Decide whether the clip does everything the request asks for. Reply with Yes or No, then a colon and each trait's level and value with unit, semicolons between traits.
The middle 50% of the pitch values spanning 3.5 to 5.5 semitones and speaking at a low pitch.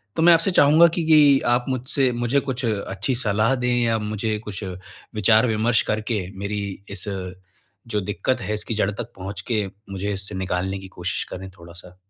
Yes: average, 4.0 semitones; low, 110 Hz